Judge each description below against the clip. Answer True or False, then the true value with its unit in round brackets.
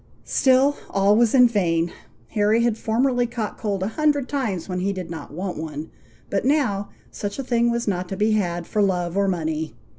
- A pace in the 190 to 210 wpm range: True (200 wpm)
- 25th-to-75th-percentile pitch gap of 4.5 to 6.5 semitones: True (4.8 semitones)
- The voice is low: False (205 Hz)